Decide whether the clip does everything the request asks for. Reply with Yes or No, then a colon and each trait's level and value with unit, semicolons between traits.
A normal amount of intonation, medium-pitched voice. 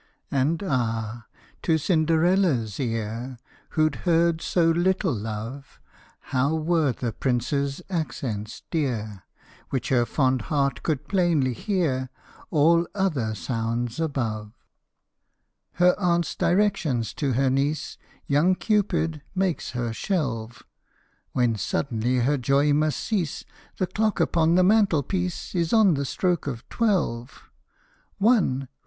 No: wide, 6.0 semitones; medium, 145 Hz